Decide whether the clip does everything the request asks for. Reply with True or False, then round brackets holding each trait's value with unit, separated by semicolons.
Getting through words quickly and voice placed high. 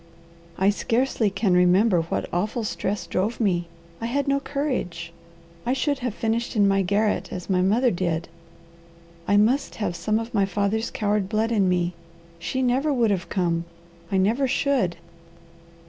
False (160 wpm; 210 Hz)